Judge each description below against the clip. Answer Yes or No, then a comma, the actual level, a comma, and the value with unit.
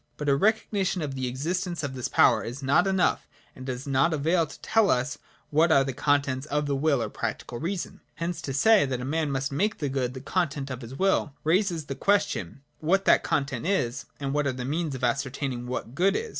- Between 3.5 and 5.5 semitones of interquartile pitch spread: Yes, average, 4.6 semitones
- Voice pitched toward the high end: No, medium, 145 Hz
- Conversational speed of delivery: No, fast, 225 wpm